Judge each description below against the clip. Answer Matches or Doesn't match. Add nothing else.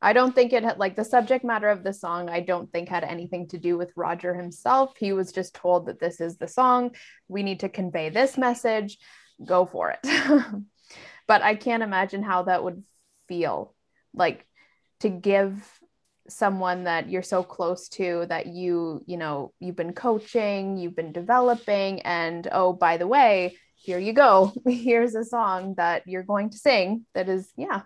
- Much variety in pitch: Doesn't match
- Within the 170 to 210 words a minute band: Matches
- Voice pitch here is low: Doesn't match